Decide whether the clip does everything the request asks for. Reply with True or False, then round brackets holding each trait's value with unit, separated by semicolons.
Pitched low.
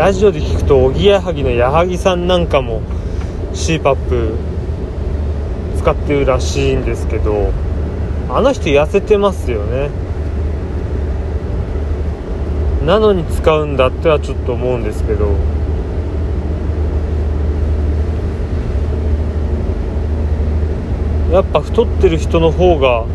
True (80 Hz)